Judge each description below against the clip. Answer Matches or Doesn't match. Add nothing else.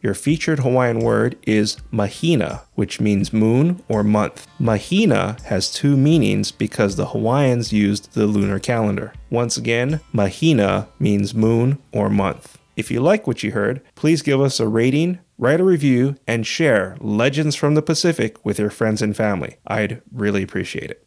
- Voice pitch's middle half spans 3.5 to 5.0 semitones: Doesn't match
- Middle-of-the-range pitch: Doesn't match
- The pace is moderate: Matches